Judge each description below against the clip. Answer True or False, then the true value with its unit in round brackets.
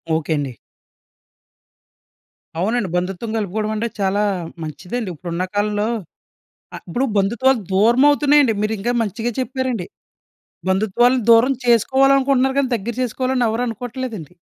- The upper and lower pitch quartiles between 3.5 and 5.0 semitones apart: True (4.7 semitones)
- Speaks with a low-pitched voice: False (230 Hz)